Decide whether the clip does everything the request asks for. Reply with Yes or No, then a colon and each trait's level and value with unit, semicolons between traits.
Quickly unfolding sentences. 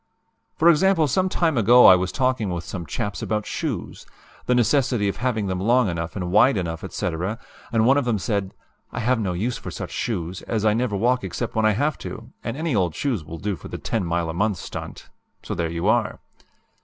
Yes: fast, 215 wpm